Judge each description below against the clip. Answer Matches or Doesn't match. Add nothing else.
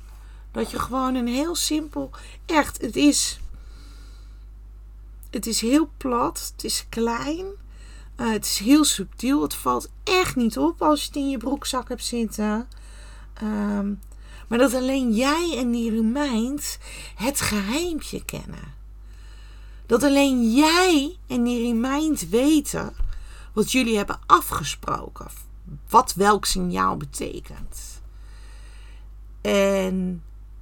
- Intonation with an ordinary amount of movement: Doesn't match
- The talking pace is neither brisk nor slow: Doesn't match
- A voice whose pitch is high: Matches